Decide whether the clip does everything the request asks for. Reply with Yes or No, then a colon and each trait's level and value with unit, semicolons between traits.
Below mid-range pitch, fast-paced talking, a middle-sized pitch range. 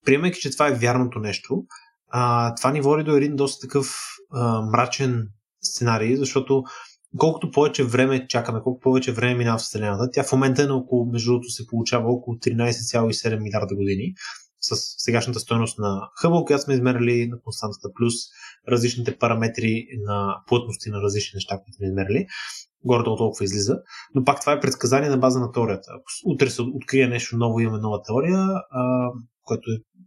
Yes: low, 120 Hz; fast, 175 wpm; average, 3.0 semitones